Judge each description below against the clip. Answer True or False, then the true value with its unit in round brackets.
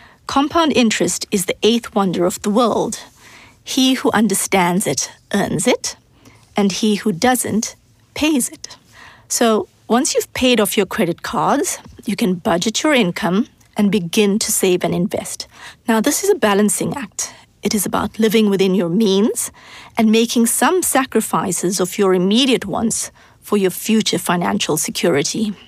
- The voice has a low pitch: False (215 Hz)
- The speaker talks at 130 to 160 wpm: True (155 wpm)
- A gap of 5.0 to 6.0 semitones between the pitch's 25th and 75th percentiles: False (3.4 semitones)